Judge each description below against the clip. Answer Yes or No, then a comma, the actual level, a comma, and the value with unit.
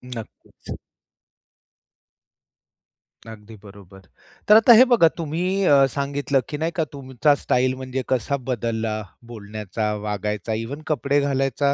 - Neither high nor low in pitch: No, low, 130 Hz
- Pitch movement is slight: No, average, 4.7 semitones